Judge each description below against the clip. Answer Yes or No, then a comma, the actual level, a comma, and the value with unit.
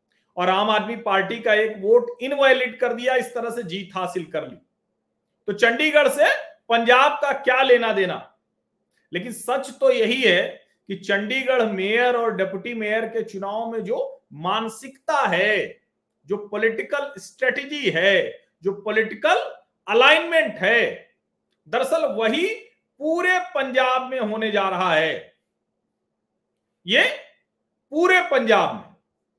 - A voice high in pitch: Yes, high, 240 Hz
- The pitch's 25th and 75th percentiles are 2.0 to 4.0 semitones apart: No, average, 4.9 semitones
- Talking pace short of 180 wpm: Yes, average, 130 wpm